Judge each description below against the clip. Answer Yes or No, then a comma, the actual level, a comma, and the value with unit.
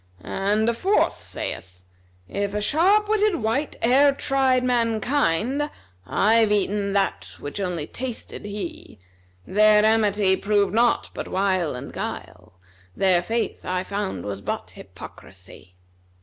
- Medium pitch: No, high, 210 Hz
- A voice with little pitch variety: No, average, 4.6 semitones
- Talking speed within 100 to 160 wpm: Yes, slow, 135 wpm